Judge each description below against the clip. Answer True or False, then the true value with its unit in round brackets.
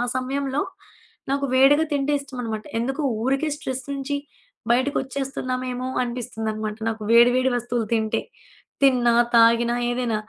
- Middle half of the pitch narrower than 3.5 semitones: True (2.6 semitones)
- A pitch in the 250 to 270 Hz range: True (255 Hz)